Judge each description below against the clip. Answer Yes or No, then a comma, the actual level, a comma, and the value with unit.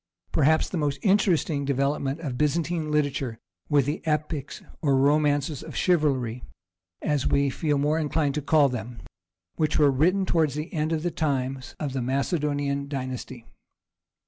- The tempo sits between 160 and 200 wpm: No, average, 150 wpm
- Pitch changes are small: Yes, narrow, 2.3 semitones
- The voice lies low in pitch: No, medium, 145 Hz